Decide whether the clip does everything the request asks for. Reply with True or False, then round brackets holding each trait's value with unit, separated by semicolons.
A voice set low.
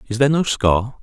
True (120 Hz)